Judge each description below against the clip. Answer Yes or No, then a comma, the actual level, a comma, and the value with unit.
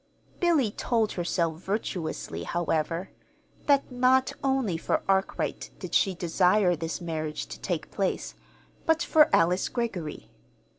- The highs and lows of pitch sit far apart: Yes, wide, 6.9 semitones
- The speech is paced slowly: Yes, slow, 120 wpm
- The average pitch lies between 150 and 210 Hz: Yes, medium, 185 Hz